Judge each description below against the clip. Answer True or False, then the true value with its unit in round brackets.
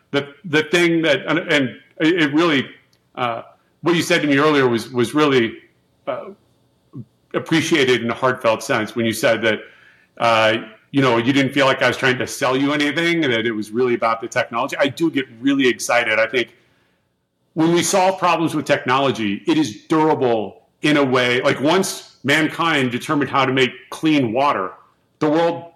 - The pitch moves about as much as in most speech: True (4.3 semitones)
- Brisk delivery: False (185 wpm)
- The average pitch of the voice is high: False (140 Hz)